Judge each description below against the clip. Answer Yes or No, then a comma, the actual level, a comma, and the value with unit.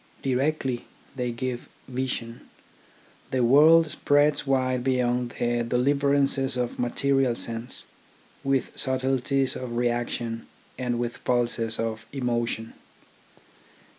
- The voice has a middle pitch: No, low, 125 Hz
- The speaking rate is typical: No, slow, 105 wpm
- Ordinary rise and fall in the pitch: No, narrow, 2.1 semitones